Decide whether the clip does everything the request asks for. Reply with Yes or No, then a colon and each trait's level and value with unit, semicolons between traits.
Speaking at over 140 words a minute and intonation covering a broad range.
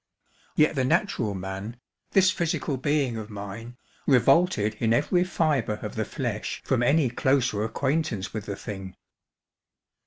No: slow, 135 wpm; wide, 6.1 semitones